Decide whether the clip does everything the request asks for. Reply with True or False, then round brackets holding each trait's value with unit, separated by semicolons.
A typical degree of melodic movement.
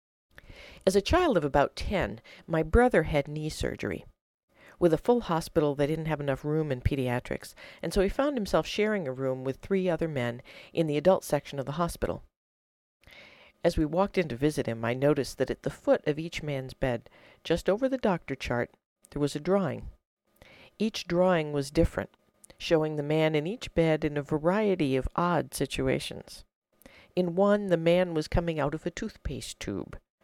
True (5.0 semitones)